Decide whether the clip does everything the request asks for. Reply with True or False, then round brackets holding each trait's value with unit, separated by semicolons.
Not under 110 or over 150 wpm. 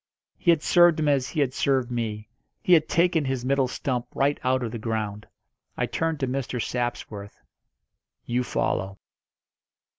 False (160 wpm)